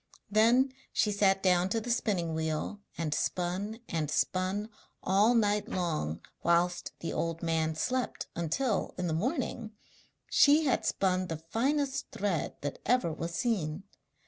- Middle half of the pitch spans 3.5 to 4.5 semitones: No, average, 5.3 semitones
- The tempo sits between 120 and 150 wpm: Yes, average, 145 wpm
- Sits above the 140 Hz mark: Yes, high, 190 Hz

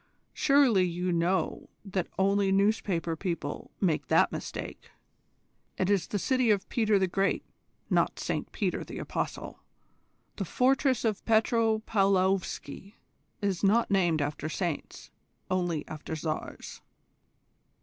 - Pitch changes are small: No, average, 3.8 semitones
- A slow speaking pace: Yes, slow, 120 wpm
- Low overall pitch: No, high, 195 Hz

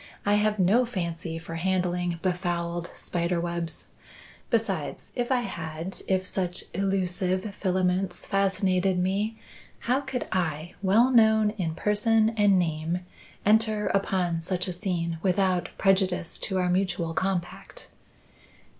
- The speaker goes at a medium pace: No, slow, 125 wpm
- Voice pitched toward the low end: No, medium, 185 Hz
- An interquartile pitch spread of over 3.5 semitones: No, average, 2.9 semitones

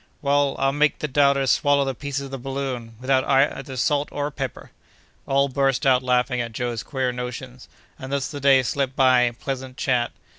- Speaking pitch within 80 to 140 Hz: Yes, low, 135 Hz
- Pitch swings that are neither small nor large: No, narrow, 1.7 semitones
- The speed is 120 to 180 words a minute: No, average, 190 wpm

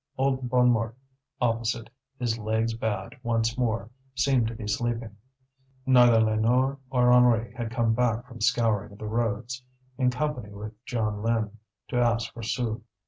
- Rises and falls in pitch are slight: Yes, narrow, 1.8 semitones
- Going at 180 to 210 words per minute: No, average, 140 wpm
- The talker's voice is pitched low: Yes, low, 115 Hz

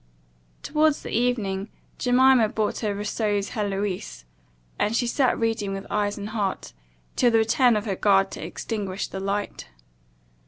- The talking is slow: No, average, 150 wpm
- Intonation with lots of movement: No, average, 2.8 semitones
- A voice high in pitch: Yes, high, 210 Hz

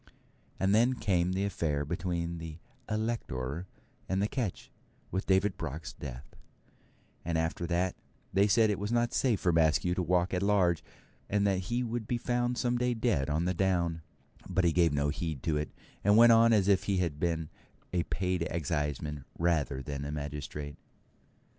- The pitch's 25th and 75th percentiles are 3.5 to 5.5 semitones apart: Yes, average, 4.6 semitones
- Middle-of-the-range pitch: No, very low, 90 Hz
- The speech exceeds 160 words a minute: Yes, average, 180 wpm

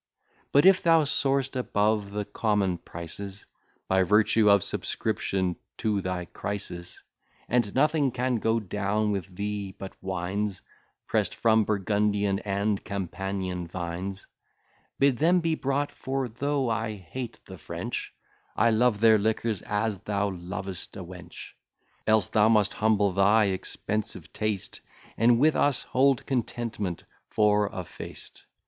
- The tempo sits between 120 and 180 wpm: Yes, slow, 135 wpm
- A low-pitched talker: Yes, low, 105 Hz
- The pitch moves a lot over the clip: No, average, 3.2 semitones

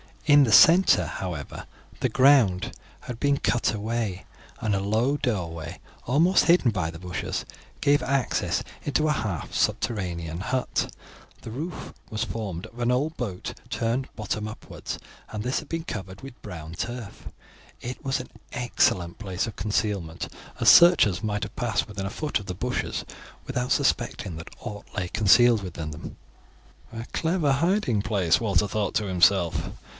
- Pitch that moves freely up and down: Yes, wide, 5.7 semitones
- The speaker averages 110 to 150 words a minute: No, average, 160 wpm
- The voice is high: No, low, 110 Hz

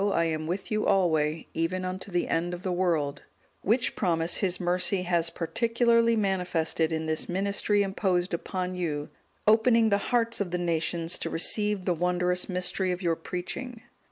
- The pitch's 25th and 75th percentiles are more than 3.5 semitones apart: No, average, 3.1 semitones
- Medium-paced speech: Yes, average, 165 wpm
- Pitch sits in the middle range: Yes, medium, 180 Hz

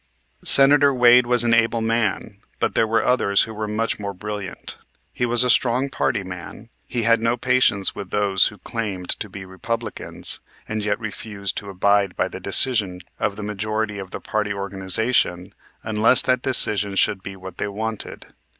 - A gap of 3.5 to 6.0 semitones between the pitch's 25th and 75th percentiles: No, average, 2.7 semitones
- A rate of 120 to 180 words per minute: Yes, average, 175 wpm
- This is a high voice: No, low, 105 Hz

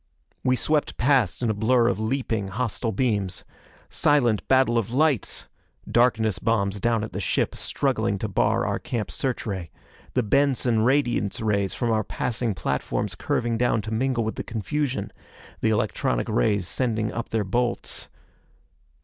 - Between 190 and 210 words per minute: No, average, 155 wpm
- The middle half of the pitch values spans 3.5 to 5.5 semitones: No, average, 3.1 semitones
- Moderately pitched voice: No, low, 115 Hz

